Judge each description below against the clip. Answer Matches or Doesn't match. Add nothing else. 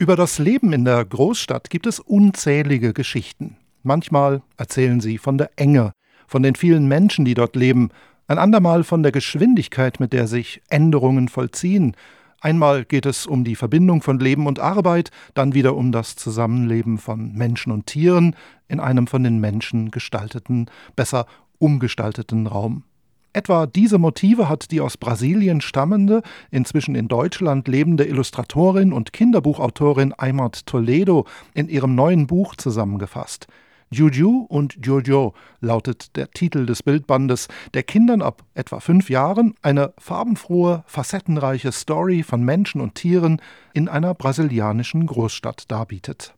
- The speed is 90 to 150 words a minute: Matches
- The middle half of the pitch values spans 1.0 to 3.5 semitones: Doesn't match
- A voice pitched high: Doesn't match